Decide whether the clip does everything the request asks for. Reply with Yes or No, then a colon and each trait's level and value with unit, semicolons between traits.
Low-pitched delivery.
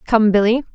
No: high, 220 Hz